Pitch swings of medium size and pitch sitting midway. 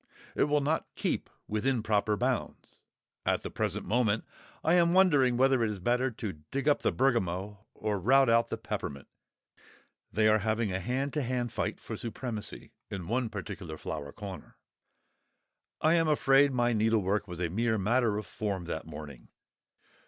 No: average, 4.5 semitones; low, 115 Hz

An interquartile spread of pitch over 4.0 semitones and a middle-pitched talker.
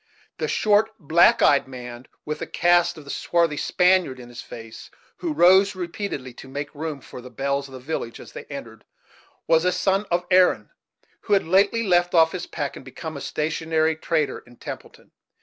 Yes: average, 4.7 semitones; medium, 160 Hz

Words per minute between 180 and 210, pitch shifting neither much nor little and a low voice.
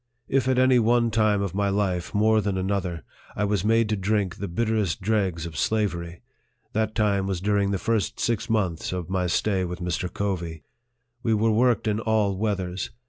Yes: average, 190 wpm; average, 3.1 semitones; low, 100 Hz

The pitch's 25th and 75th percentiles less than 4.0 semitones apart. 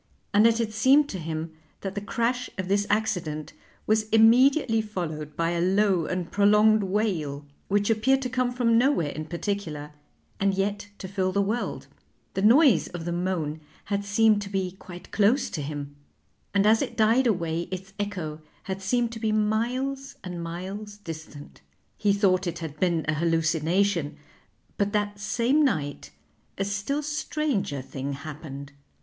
No: average, 4.8 semitones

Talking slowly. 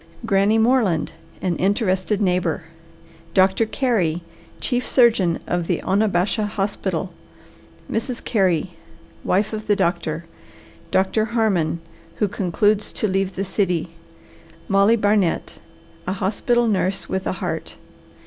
Yes: slow, 115 wpm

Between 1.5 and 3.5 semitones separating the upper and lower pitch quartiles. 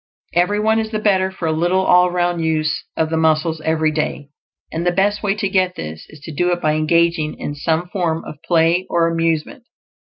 Yes: average, 2.8 semitones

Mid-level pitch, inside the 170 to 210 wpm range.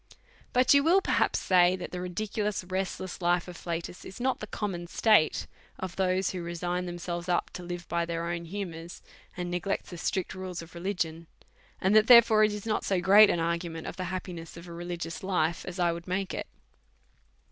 Yes: medium, 180 Hz; fast, 205 wpm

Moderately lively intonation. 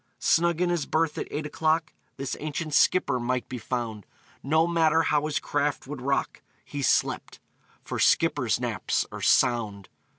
Yes: average, 4.0 semitones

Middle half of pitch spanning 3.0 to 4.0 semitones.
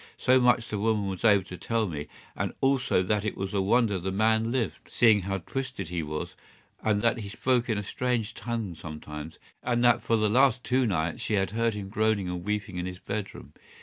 Yes: average, 3.5 semitones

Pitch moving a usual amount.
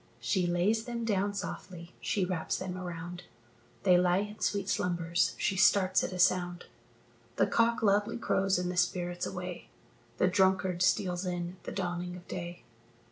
No: narrow, 1.7 semitones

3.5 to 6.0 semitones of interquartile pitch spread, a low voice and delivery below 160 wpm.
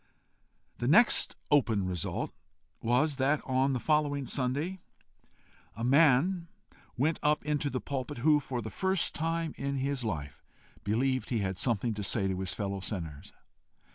Yes: average, 5.3 semitones; low, 130 Hz; average, 150 wpm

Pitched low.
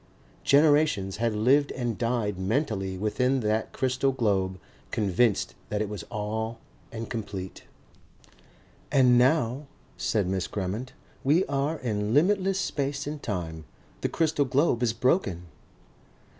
Yes: low, 115 Hz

